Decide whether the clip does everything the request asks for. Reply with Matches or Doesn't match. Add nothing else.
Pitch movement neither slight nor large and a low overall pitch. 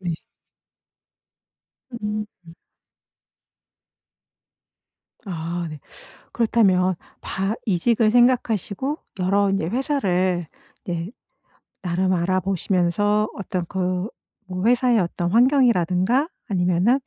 Doesn't match